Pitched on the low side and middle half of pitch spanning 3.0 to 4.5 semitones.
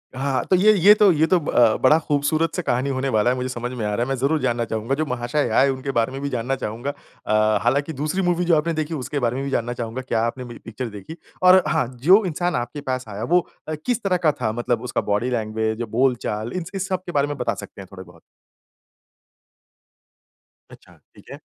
No: low, 130 Hz; average, 5.0 semitones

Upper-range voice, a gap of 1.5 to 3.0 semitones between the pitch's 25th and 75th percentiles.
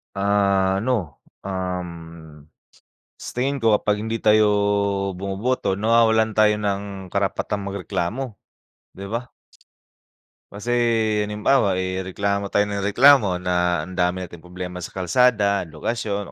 No: low, 100 Hz; average, 2.7 semitones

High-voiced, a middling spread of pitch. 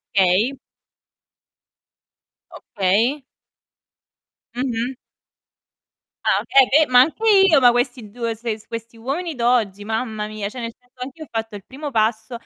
Yes: high, 240 Hz; average, 3.2 semitones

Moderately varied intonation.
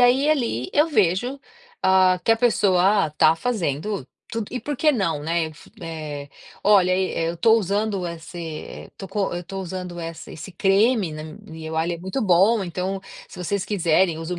Yes: average, 4.3 semitones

